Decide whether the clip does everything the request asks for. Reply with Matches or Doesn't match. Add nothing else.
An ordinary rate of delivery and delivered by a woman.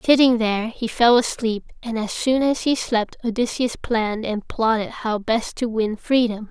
Matches